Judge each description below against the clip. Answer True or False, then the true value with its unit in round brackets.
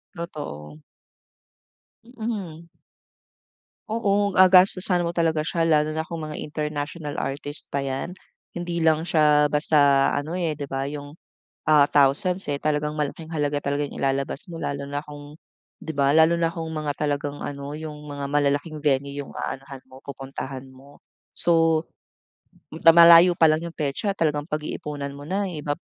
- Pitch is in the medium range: True (150 Hz)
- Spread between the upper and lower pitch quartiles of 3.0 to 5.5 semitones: False (2.6 semitones)